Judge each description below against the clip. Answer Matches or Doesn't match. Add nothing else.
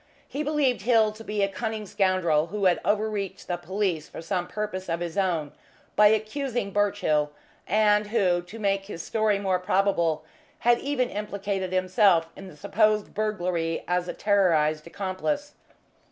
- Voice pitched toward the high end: Matches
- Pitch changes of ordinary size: Matches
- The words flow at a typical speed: Matches